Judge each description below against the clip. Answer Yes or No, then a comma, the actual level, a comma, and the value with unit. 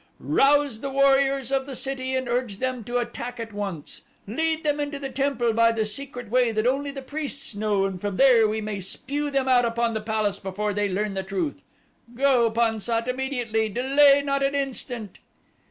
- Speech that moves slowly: No, average, 195 wpm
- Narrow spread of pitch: No, average, 4.1 semitones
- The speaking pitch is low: No, high, 245 Hz